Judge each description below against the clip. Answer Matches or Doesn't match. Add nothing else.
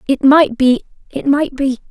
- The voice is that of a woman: Matches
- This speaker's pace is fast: Doesn't match